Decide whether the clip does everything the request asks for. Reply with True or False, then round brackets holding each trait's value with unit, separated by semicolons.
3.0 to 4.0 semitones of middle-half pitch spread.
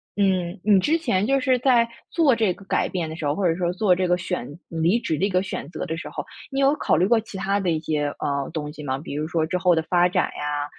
False (4.4 semitones)